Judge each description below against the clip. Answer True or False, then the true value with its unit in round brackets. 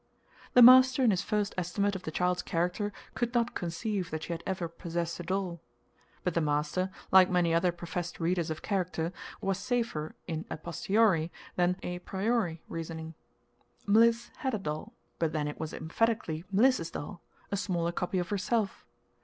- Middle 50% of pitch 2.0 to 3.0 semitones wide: False (3.7 semitones)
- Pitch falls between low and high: True (180 Hz)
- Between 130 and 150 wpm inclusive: False (170 wpm)